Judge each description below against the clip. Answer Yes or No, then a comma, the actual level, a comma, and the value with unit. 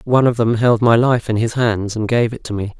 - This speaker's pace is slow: No, fast, 300 wpm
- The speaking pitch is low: Yes, low, 115 Hz